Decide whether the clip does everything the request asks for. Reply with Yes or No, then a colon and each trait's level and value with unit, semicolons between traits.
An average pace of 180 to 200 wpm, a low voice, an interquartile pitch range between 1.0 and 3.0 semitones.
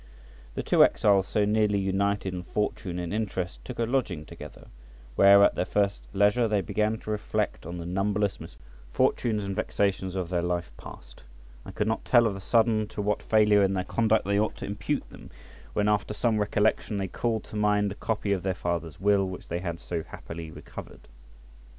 Yes: average, 195 wpm; low, 100 Hz; narrow, 2.5 semitones